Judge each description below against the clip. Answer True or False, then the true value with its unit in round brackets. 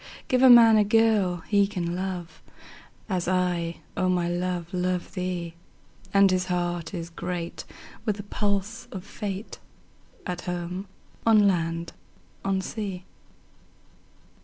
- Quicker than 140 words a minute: False (135 wpm)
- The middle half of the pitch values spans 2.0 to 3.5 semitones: True (2.5 semitones)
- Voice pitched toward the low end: False (185 Hz)